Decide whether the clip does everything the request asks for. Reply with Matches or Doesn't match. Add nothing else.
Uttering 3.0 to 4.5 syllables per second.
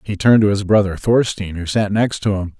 Doesn't match